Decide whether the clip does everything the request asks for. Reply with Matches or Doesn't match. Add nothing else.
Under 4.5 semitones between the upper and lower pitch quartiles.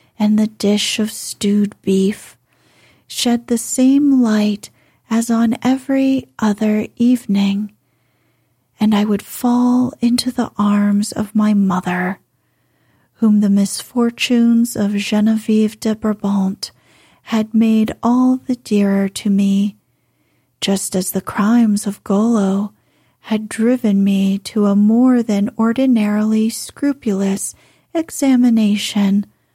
Matches